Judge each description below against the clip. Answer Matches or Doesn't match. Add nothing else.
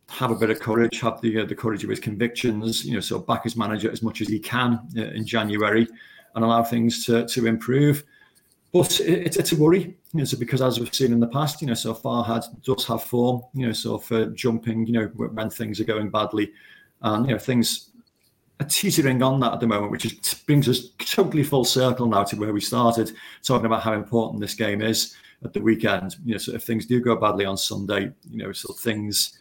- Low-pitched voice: Matches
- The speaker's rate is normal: Doesn't match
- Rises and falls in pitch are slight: Matches